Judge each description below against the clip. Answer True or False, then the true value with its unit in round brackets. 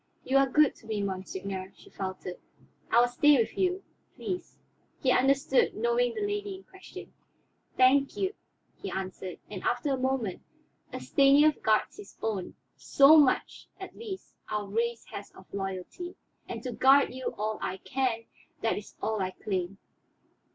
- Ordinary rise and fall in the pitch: False (7.0 semitones)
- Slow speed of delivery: False (160 wpm)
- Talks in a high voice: True (250 Hz)